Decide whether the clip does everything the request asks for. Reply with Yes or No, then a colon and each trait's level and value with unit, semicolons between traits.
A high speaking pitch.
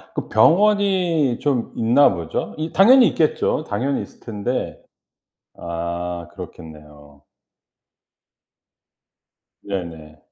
No: low, 115 Hz